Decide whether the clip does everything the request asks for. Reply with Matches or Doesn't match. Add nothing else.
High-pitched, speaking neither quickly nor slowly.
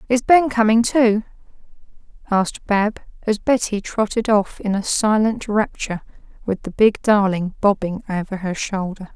Matches